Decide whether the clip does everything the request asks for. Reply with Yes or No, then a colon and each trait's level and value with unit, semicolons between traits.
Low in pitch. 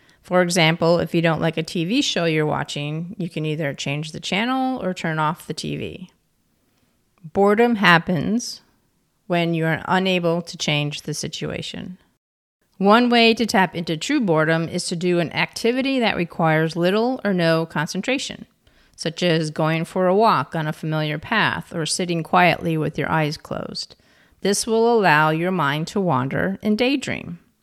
No: medium, 170 Hz